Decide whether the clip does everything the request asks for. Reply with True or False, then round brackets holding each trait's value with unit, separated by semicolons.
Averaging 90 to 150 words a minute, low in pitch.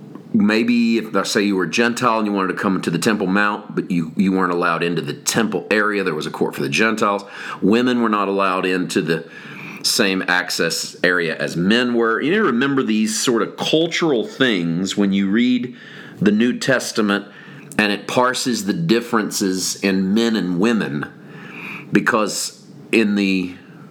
False (180 wpm; 105 Hz)